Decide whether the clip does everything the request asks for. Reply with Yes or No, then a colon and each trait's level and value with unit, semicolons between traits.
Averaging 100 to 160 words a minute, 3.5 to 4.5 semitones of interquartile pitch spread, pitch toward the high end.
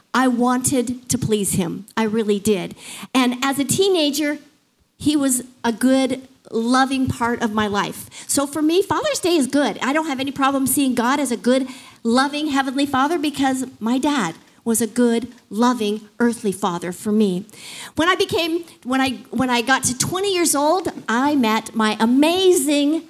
No: average, 175 wpm; average, 3.8 semitones; very high, 260 Hz